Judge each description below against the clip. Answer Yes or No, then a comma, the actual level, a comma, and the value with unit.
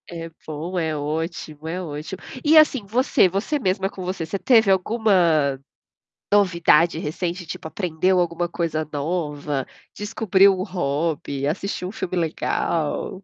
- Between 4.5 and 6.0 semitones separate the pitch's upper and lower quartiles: No, average, 3.6 semitones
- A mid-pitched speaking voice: Yes, medium, 175 Hz